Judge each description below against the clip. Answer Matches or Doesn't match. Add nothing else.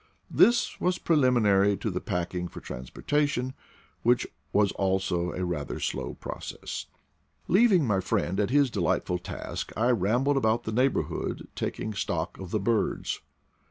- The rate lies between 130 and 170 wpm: Matches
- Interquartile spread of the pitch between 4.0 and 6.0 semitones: Matches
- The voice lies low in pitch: Matches